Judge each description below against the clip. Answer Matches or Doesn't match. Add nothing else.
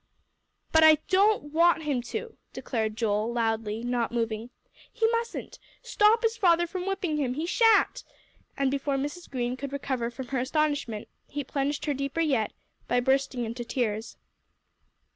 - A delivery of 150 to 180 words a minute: Matches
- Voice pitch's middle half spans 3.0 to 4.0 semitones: Doesn't match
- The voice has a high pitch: Matches